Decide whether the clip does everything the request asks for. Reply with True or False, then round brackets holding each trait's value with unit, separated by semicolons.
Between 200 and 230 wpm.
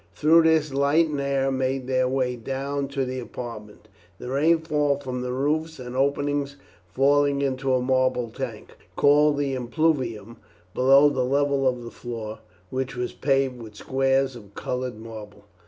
False (155 wpm)